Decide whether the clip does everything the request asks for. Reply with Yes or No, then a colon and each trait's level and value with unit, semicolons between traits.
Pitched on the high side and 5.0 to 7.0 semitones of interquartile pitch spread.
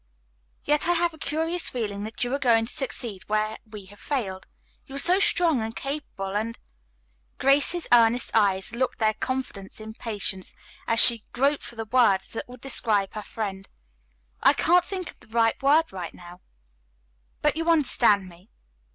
Yes: high, 230 Hz; wide, 5.4 semitones